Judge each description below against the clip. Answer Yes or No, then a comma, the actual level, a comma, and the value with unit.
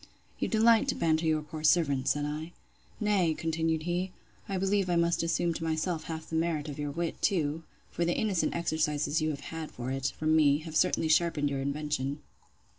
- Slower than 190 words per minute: No, average, 195 wpm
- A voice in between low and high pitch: Yes, medium, 160 Hz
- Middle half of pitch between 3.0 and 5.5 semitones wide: No, narrow, 2.4 semitones